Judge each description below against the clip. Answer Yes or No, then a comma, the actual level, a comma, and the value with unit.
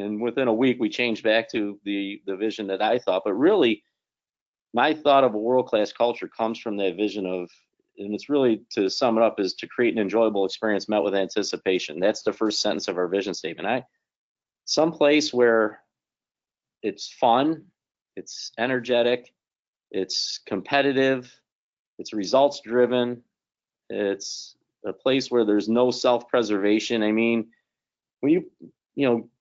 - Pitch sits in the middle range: No, low, 115 Hz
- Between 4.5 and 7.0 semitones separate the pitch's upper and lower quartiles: No, average, 3.1 semitones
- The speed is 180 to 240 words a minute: No, average, 160 wpm